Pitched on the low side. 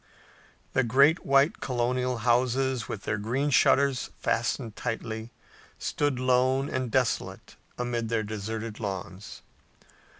Yes: low, 125 Hz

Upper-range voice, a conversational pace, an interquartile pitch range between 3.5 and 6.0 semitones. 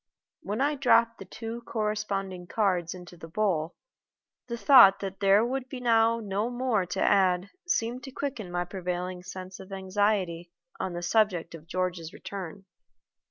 Yes: high, 195 Hz; average, 160 wpm; average, 4.0 semitones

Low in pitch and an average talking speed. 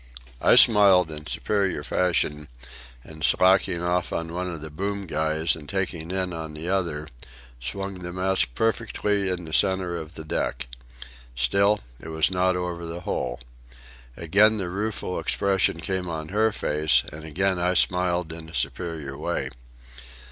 Yes: very low, 90 Hz; average, 155 wpm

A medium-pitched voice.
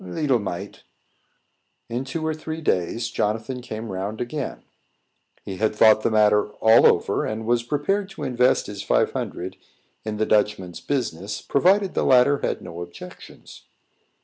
No: low, 110 Hz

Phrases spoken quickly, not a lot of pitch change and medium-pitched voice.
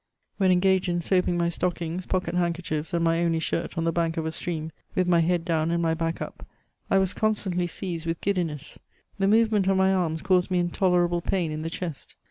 Yes: fast, 220 wpm; narrow, 2.0 semitones; medium, 175 Hz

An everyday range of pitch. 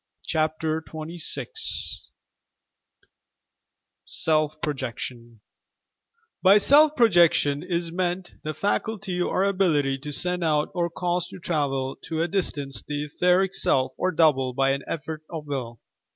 Yes: average, 3.8 semitones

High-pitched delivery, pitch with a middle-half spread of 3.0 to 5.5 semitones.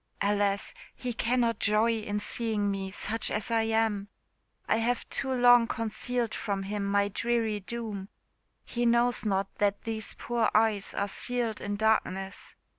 No: high, 220 Hz; narrow, 2.4 semitones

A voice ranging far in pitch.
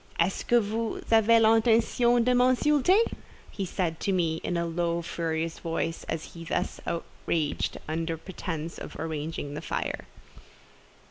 Yes: wide, 5.7 semitones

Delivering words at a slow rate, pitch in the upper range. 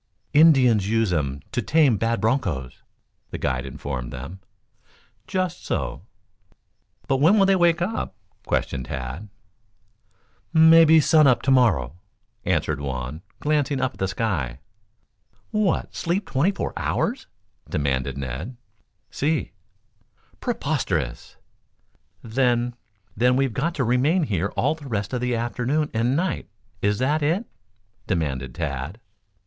No: slow, 125 wpm; low, 120 Hz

